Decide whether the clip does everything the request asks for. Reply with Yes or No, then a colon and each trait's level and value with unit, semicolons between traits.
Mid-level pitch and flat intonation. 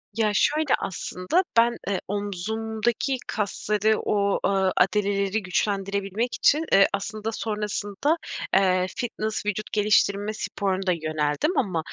No: high, 205 Hz; narrow, 2.1 semitones